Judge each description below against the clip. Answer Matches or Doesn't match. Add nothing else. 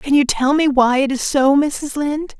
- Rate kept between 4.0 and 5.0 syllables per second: Matches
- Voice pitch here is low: Doesn't match